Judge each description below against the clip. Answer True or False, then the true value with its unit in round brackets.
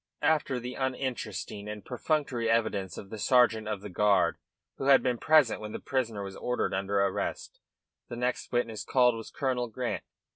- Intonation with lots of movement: False (3.4 semitones)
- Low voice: True (120 Hz)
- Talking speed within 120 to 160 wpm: False (175 wpm)